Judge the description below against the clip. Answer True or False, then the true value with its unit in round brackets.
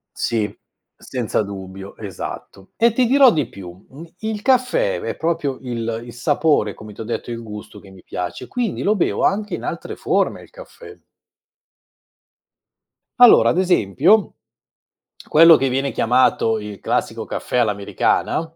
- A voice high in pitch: False (130 Hz)